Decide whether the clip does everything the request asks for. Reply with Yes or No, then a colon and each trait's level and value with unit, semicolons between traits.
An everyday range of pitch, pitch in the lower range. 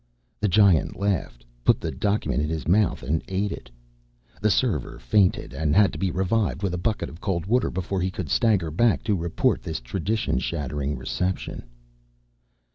Yes: average, 4.8 semitones; very low, 90 Hz